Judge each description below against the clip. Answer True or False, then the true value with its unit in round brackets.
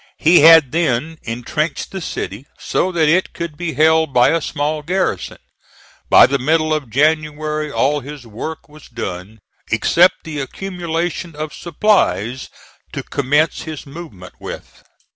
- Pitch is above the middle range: False (155 Hz)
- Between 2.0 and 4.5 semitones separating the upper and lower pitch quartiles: True (3.1 semitones)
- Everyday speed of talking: True (145 wpm)